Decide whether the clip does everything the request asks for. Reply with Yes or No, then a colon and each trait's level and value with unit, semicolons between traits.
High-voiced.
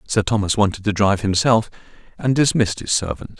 No: low, 105 Hz